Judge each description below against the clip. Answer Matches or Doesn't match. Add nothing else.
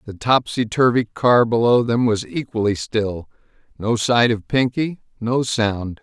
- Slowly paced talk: Doesn't match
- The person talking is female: Doesn't match